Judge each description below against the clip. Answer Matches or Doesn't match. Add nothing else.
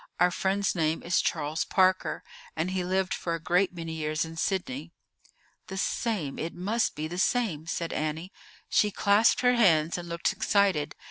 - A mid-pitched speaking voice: Matches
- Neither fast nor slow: Matches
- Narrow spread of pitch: Doesn't match